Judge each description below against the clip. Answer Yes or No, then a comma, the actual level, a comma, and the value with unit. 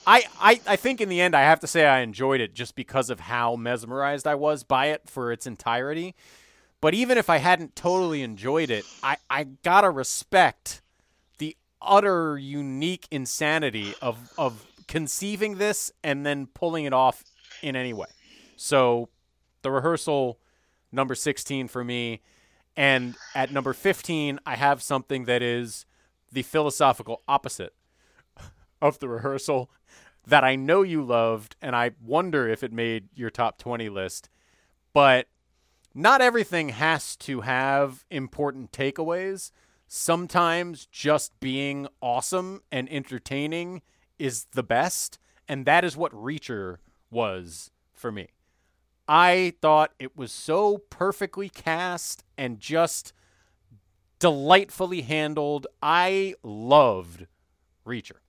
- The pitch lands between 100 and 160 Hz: Yes, low, 135 Hz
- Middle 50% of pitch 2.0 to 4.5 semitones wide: No, average, 5.3 semitones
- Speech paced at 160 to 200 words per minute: No, slow, 135 wpm